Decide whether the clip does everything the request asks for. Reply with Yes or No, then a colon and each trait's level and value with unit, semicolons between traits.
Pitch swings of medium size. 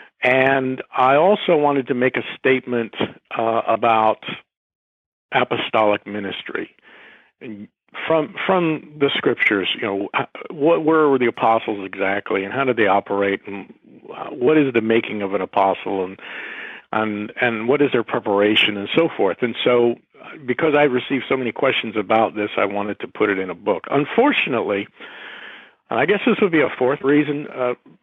Yes: average, 4.4 semitones